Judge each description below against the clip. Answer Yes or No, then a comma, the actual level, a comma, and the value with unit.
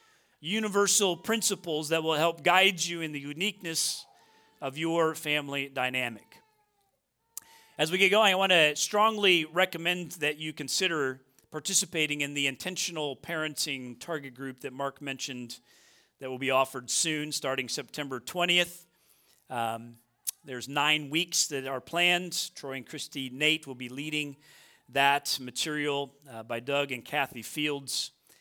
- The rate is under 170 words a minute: Yes, average, 140 wpm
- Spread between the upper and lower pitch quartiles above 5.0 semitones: No, average, 4.1 semitones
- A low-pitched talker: No, medium, 150 Hz